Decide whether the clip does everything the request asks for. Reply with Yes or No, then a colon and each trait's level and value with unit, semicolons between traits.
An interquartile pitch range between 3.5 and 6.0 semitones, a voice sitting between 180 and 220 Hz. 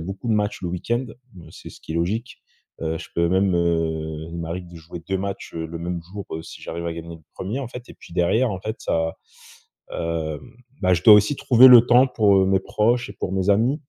No: average, 4.4 semitones; very low, 95 Hz